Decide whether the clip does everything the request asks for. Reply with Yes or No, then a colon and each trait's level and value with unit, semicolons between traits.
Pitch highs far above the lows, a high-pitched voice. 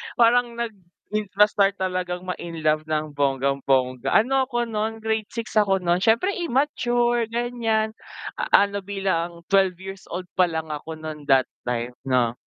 Yes: wide, 6.2 semitones; high, 195 Hz